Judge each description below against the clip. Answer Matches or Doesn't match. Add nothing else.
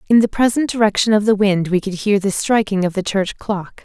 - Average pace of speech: Doesn't match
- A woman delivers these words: Matches